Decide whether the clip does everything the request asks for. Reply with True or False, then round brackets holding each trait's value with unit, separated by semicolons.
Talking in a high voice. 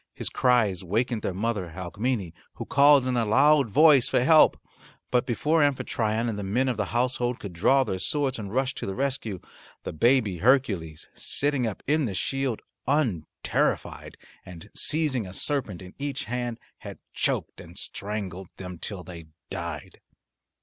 False (115 Hz)